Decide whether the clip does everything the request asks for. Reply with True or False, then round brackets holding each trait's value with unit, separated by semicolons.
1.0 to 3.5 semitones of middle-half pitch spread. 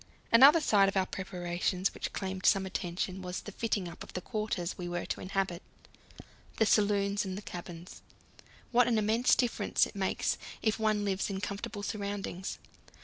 True (2.5 semitones)